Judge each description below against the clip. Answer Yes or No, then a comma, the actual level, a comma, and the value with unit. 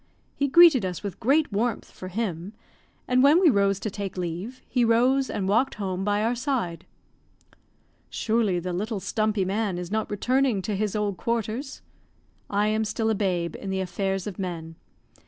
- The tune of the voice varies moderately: Yes, average, 3.7 semitones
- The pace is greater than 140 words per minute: Yes, average, 175 wpm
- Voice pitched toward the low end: No, high, 210 Hz